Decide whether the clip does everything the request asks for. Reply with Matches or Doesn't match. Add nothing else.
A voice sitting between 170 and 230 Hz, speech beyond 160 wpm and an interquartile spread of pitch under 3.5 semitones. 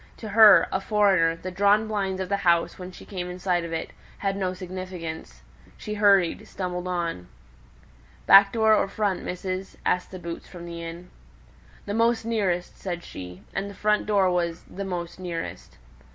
Matches